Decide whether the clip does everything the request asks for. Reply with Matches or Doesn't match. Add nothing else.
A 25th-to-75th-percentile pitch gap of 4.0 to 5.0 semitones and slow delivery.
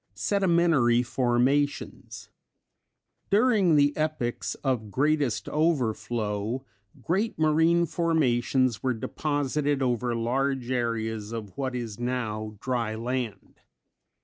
Matches